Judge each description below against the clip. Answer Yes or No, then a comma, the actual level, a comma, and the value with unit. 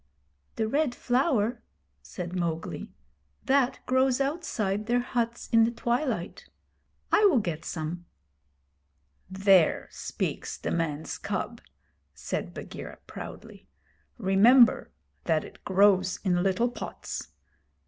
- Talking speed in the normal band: No, slow, 105 wpm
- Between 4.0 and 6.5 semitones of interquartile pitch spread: Yes, average, 5.0 semitones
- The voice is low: No, high, 220 Hz